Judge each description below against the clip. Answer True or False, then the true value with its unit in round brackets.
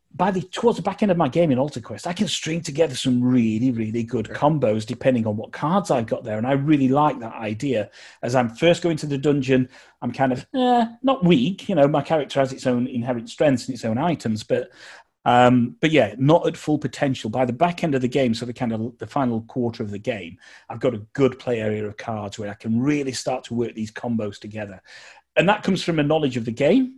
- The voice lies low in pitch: True (130 Hz)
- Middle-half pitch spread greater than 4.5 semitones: True (5.0 semitones)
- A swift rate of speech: True (250 wpm)